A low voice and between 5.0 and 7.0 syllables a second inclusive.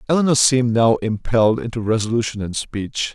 Yes: low, 115 Hz; 5.8 syllables/s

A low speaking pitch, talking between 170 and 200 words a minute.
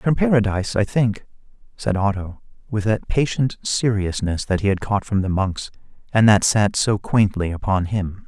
Yes: low, 105 Hz; average, 175 wpm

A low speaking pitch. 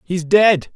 No: medium, 180 Hz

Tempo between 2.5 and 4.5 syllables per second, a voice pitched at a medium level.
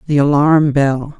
Yes: 3.9 syllables/s; medium, 145 Hz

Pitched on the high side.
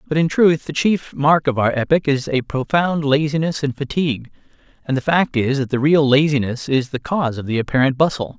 No: medium, 145 Hz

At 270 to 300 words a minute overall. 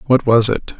No: fast, 225 wpm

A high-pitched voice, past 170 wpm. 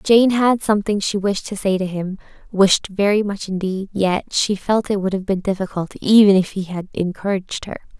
Yes: high, 195 Hz; average, 195 wpm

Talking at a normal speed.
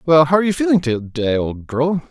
No: fast, 255 wpm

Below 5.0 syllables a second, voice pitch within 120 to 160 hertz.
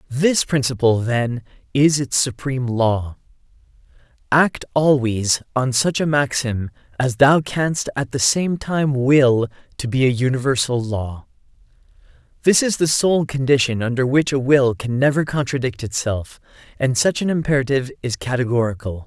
Yes: 4.6 syllables/s; low, 130 Hz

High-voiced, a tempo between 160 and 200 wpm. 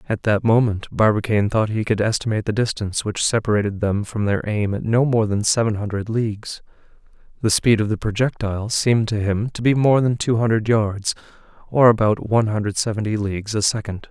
No: low, 110 Hz; average, 195 wpm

